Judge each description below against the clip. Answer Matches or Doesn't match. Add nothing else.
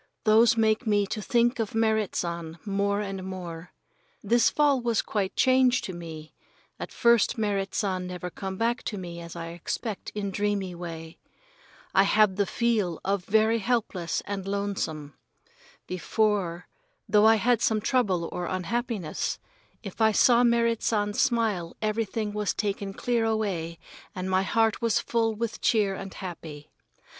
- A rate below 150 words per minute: Doesn't match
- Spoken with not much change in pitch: Doesn't match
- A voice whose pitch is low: Doesn't match